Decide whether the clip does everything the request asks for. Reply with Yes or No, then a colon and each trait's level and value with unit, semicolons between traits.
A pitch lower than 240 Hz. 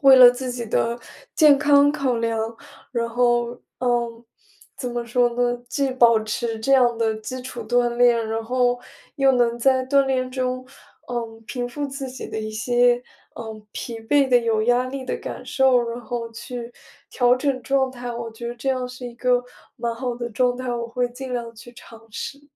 No: high, 245 Hz